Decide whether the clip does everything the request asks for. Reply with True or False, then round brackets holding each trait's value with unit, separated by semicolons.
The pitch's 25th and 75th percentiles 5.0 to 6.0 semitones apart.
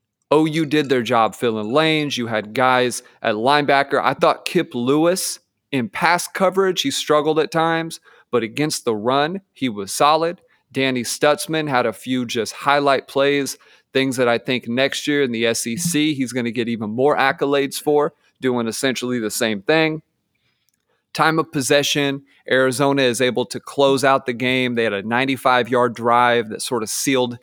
False (3.5 semitones)